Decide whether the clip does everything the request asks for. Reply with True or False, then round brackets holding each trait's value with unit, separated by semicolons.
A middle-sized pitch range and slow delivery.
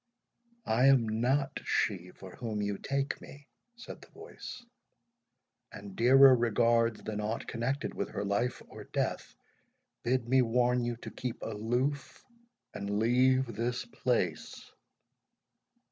True (3.1 semitones; 130 wpm)